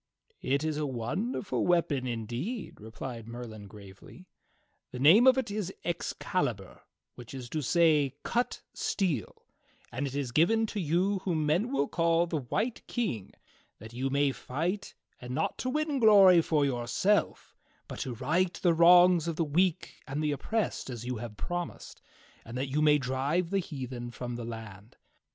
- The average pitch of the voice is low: No, medium, 150 Hz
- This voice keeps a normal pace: Yes, average, 165 wpm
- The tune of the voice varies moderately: No, wide, 6.6 semitones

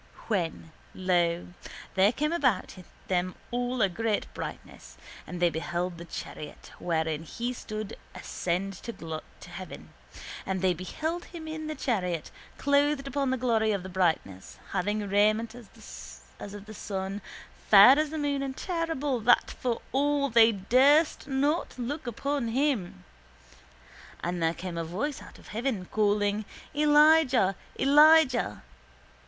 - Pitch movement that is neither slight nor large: No, wide, 7.3 semitones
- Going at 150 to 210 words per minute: No, average, 140 wpm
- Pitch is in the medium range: No, high, 220 Hz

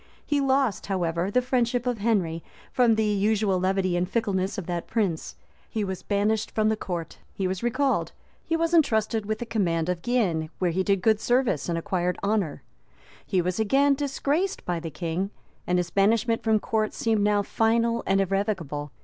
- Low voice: No, high, 205 Hz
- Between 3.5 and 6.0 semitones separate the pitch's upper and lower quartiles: Yes, average, 4.2 semitones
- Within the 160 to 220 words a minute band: Yes, average, 180 wpm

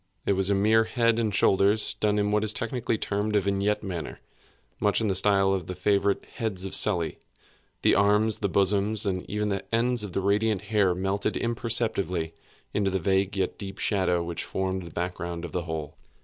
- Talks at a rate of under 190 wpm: No, average, 200 wpm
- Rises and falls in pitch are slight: Yes, narrow, 2.1 semitones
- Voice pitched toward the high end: No, low, 100 Hz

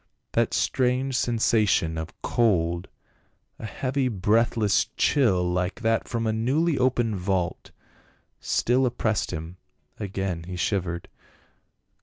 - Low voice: Yes, low, 110 Hz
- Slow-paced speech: Yes, slow, 110 wpm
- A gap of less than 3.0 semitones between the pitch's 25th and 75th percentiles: No, average, 5.2 semitones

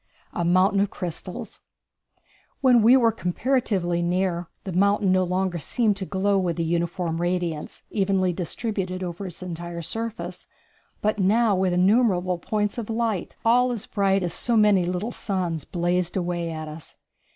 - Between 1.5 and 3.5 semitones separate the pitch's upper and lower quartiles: Yes, average, 3.2 semitones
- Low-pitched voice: No, medium, 185 Hz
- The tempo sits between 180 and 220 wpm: No, average, 150 wpm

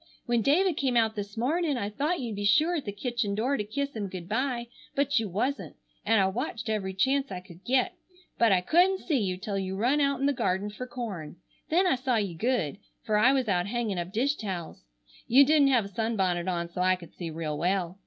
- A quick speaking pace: Yes, fast, 235 wpm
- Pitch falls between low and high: No, high, 220 Hz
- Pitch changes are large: Yes, wide, 5.9 semitones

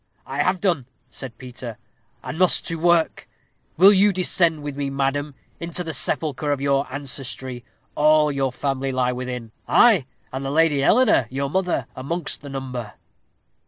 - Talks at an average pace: Yes, average, 160 wpm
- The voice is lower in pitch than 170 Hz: Yes, medium, 140 Hz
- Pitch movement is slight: No, average, 3.8 semitones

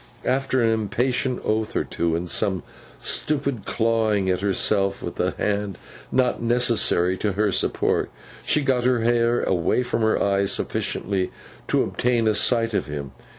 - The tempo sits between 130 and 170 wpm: Yes, average, 155 wpm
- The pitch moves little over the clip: No, average, 3.7 semitones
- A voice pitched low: Yes, low, 110 Hz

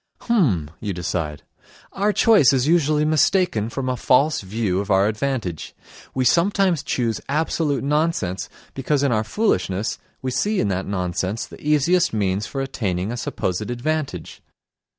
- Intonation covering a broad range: Yes, wide, 7.7 semitones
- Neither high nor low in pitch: No, low, 125 Hz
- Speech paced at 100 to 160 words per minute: Yes, average, 150 wpm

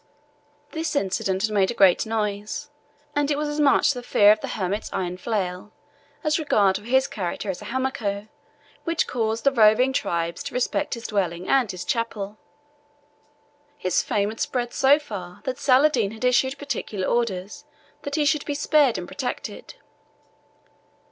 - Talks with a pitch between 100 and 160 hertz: No, high, 225 Hz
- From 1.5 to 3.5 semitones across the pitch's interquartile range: No, average, 5.3 semitones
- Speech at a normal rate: Yes, average, 165 wpm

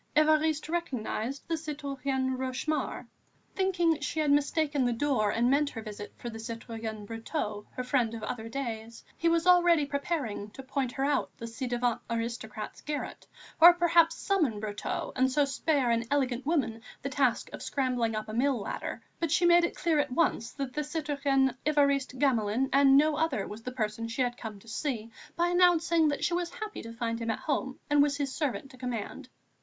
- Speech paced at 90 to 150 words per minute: No, average, 190 wpm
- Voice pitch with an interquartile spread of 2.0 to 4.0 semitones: No, average, 4.8 semitones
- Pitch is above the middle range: Yes, very high, 270 Hz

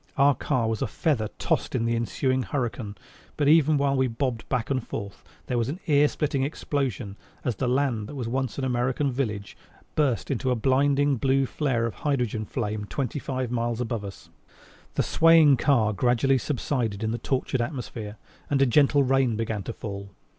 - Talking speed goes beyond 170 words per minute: Yes, average, 190 wpm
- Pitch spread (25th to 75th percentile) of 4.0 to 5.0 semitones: No, average, 3.4 semitones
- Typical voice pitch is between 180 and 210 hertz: No, low, 125 Hz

